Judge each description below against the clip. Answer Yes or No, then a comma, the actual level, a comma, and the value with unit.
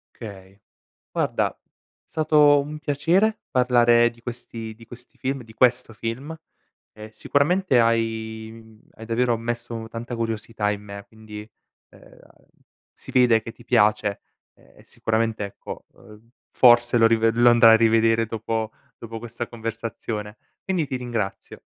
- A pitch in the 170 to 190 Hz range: No, low, 115 Hz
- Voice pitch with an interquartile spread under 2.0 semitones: Yes, narrow, 1.6 semitones